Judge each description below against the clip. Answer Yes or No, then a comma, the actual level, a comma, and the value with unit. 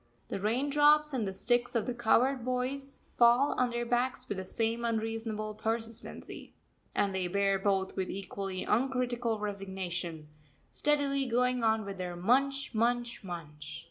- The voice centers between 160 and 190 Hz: No, high, 230 Hz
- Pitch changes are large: No, average, 4.2 semitones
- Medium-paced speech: Yes, average, 145 wpm